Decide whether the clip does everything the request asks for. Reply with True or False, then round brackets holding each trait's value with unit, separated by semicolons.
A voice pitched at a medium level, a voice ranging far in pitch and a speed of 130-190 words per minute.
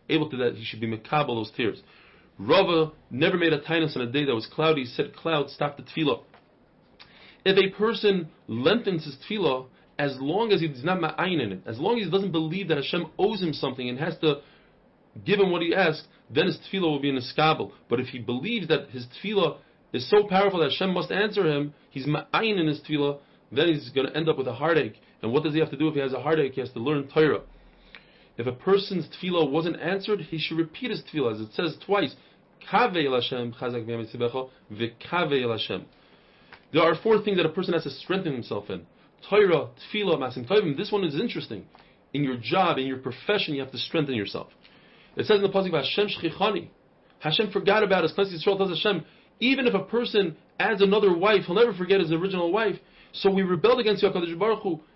False (160 Hz; 5.7 semitones; 205 wpm)